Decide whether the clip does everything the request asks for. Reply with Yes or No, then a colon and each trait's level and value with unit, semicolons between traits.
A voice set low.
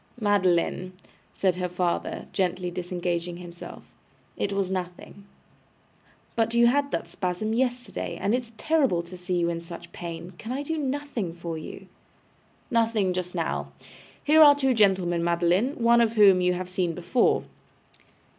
No: medium, 185 Hz